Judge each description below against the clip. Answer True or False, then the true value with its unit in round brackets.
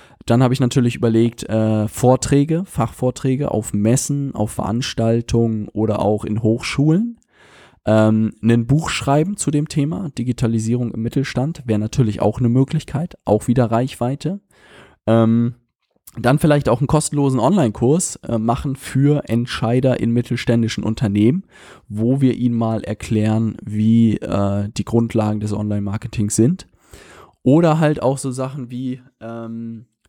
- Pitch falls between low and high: False (120 Hz)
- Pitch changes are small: False (3.5 semitones)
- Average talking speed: True (135 wpm)